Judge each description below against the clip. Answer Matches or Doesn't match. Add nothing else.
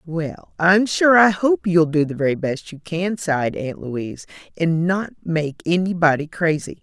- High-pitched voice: Doesn't match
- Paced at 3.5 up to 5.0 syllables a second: Matches